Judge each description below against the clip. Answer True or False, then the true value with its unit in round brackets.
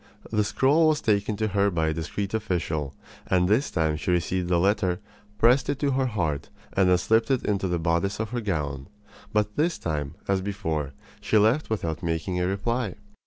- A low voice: True (100 Hz)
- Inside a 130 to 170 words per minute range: False (195 wpm)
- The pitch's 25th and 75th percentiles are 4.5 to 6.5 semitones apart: True (5.0 semitones)